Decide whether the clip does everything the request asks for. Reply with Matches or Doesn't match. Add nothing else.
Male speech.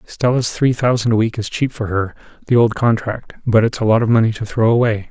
Matches